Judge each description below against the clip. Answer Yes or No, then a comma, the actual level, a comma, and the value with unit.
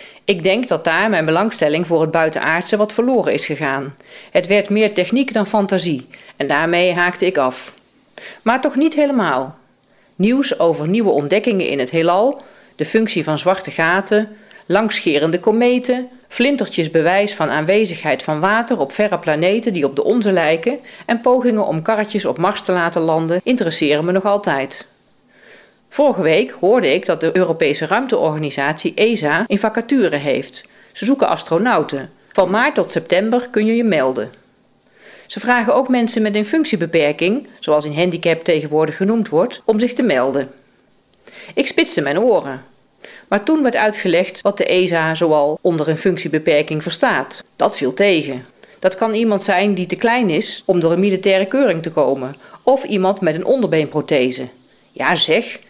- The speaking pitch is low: No, high, 190 Hz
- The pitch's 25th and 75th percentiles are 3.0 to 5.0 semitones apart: No, wide, 5.5 semitones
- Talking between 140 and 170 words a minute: Yes, average, 160 wpm